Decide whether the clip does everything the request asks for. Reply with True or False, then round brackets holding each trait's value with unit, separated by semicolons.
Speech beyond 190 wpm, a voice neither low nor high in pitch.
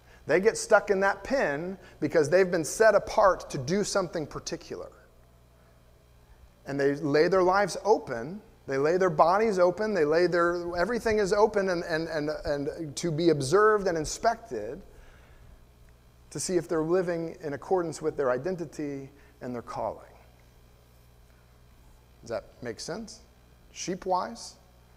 False (140 wpm; 155 Hz)